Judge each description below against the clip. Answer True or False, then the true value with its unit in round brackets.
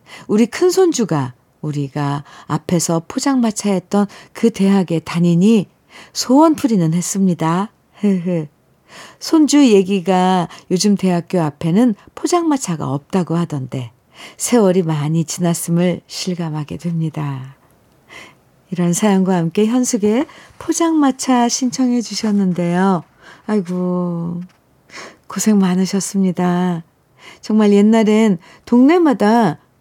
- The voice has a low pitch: False (185 Hz)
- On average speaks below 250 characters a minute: True (235 characters per minute)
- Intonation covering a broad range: False (5.0 semitones)